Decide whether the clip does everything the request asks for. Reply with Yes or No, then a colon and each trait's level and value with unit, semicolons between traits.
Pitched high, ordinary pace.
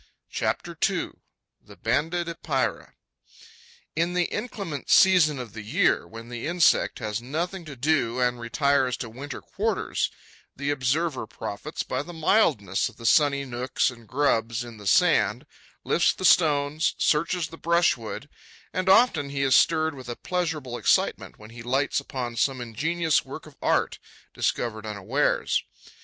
No: medium, 140 Hz; average, 150 wpm